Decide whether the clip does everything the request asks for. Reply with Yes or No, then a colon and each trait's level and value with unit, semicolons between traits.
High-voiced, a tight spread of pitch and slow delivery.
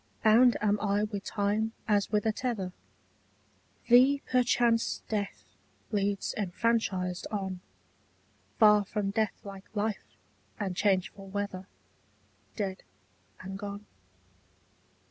Yes: high, 205 Hz; narrow, 2.0 semitones; slow, 100 wpm